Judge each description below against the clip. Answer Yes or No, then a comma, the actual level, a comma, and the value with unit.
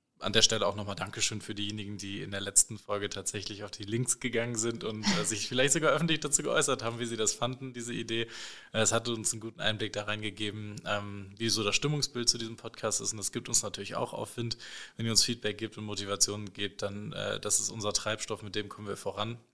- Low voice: Yes, low, 110 Hz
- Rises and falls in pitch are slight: Yes, narrow, 2.1 semitones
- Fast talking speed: Yes, fast, 235 wpm